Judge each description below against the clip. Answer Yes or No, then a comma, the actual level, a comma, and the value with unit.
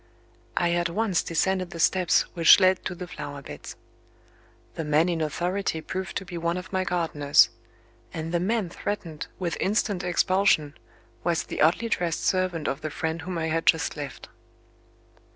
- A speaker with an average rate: Yes, average, 170 wpm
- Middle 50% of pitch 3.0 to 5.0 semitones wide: No, narrow, 2.5 semitones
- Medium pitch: Yes, medium, 170 Hz